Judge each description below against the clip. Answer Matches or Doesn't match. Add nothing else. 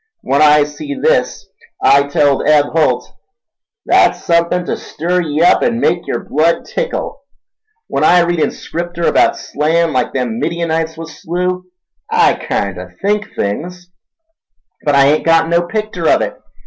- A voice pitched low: Doesn't match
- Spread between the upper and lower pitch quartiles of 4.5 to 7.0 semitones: Doesn't match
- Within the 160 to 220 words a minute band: Doesn't match